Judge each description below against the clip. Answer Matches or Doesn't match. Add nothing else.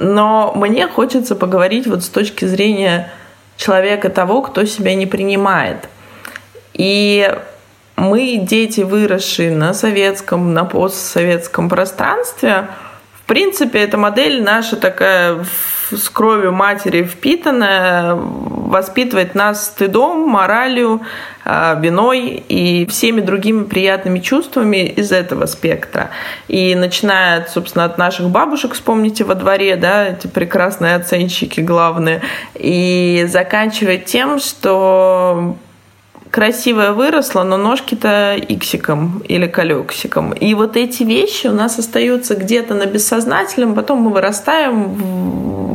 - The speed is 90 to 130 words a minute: Matches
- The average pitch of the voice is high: Matches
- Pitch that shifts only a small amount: Doesn't match